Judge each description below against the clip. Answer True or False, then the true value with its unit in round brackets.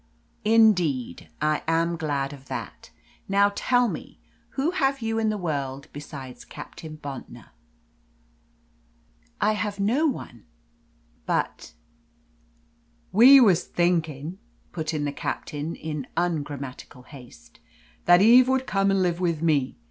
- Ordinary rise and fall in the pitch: False (6.5 semitones)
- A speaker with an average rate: False (125 wpm)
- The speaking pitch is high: False (165 Hz)